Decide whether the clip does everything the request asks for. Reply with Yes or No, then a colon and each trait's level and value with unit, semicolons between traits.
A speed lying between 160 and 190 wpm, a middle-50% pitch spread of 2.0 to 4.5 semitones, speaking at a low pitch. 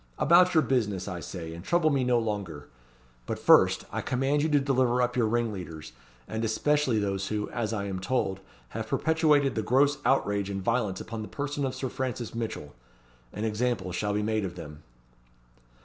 No: average, 185 wpm; average, 5.0 semitones; low, 115 Hz